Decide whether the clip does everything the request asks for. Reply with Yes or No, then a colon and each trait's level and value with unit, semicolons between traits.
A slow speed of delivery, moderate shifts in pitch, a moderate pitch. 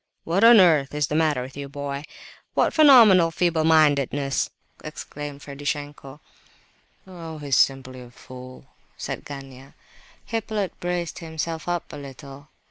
Yes: slow, 130 wpm; average, 3.6 semitones; medium, 145 Hz